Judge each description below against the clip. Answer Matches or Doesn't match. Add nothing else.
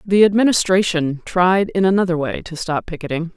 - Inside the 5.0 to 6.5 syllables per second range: Matches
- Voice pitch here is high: Doesn't match